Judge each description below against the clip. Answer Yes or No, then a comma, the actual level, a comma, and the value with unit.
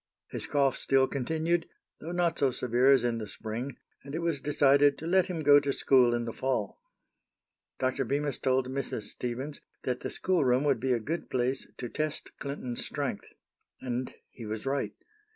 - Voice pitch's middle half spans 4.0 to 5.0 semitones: No, average, 2.8 semitones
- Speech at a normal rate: Yes, average, 180 wpm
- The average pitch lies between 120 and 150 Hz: Yes, low, 135 Hz